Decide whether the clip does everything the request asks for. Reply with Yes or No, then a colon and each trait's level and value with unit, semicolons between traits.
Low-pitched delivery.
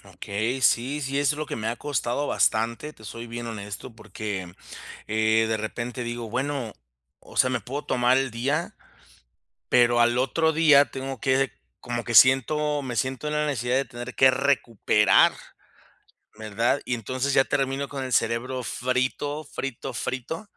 Yes: low, 125 Hz